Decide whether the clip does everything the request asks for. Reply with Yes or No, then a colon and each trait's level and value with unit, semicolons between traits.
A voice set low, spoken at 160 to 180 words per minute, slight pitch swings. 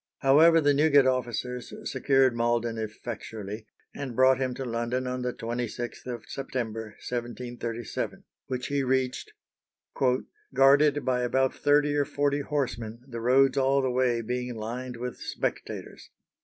No: low, 125 Hz; slow, 135 wpm; narrow, 2.3 semitones